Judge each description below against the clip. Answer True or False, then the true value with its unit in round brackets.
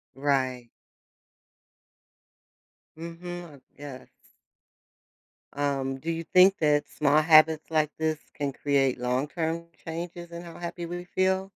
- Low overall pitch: False (155 Hz)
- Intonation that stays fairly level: False (3.2 semitones)